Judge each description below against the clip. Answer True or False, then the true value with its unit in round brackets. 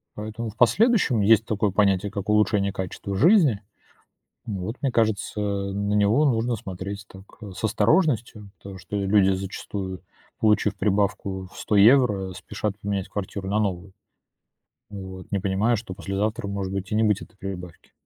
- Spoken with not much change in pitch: True (2.0 semitones)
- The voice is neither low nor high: False (100 Hz)